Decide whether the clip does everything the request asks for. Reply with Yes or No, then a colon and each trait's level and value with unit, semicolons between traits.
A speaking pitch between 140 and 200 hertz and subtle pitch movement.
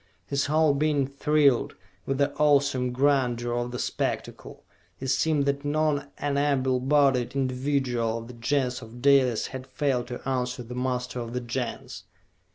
No: low, 130 Hz; narrow, 2.3 semitones